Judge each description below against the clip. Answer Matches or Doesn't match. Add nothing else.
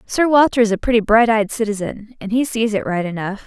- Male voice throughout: Doesn't match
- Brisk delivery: Matches